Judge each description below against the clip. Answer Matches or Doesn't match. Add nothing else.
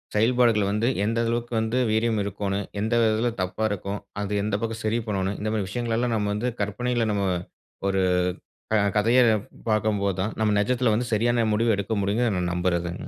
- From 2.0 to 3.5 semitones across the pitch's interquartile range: Matches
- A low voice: Matches